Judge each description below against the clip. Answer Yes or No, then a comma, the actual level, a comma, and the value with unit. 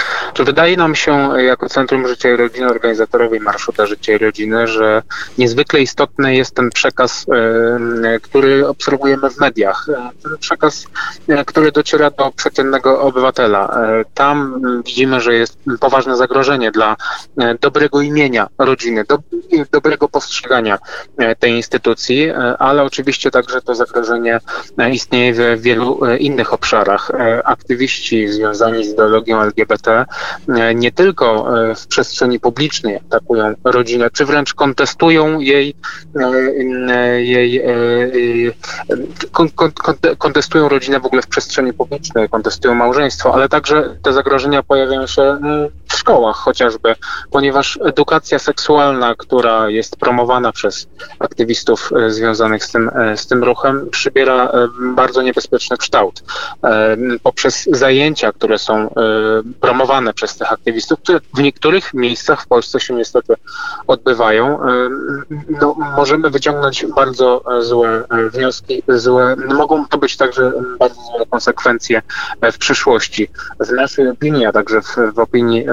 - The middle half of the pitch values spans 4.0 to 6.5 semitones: No, average, 3.2 semitones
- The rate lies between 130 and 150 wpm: No, average, 120 wpm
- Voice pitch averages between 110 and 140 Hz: Yes, low, 130 Hz